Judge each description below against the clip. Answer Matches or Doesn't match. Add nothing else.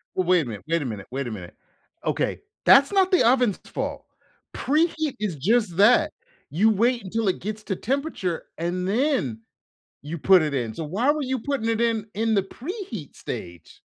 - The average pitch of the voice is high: Matches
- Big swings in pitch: Matches